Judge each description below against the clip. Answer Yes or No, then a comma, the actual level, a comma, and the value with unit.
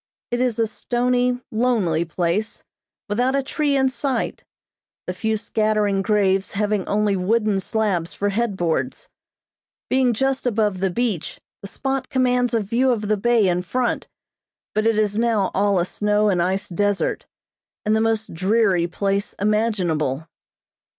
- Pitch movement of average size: Yes, average, 3.6 semitones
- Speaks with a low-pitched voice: No, high, 215 Hz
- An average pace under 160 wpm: Yes, average, 150 wpm